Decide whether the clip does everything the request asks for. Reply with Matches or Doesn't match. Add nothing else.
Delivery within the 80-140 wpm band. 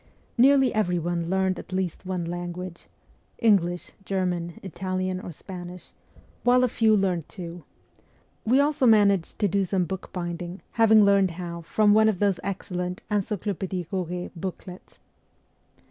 Matches